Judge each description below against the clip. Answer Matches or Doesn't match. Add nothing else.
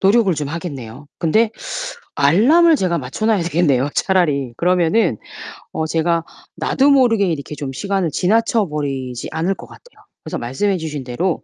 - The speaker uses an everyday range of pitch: Doesn't match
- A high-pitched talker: Doesn't match